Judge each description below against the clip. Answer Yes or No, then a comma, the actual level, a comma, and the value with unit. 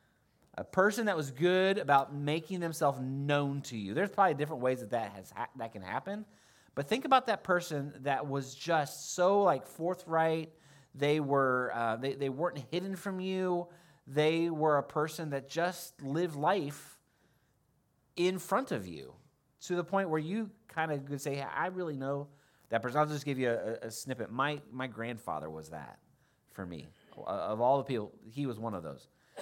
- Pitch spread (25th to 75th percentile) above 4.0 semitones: Yes, average, 4.5 semitones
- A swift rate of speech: No, average, 190 wpm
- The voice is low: No, medium, 145 Hz